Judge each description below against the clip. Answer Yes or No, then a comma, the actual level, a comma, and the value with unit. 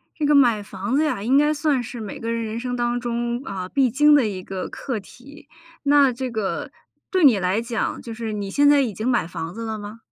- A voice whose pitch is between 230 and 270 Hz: Yes, high, 235 Hz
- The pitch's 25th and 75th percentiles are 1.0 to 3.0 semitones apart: No, average, 4.5 semitones